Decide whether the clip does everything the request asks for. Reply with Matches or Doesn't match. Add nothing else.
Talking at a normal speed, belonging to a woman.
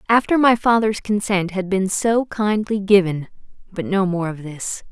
Matches